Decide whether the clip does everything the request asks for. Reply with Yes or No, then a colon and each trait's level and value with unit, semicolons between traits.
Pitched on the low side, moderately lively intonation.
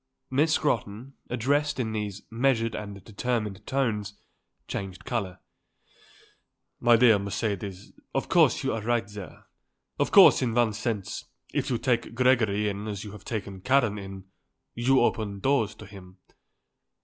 Yes: low, 110 Hz; average, 3.4 semitones